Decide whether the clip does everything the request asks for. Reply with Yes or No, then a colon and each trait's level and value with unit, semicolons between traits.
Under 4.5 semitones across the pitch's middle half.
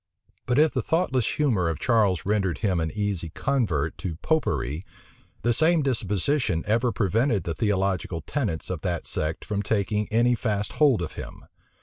No: wide, 5.4 semitones